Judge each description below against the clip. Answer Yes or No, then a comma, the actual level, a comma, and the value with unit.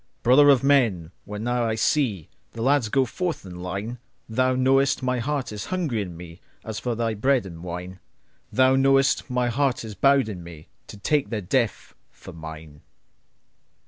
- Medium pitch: No, low, 115 Hz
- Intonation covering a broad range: Yes, wide, 5.9 semitones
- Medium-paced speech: Yes, average, 155 wpm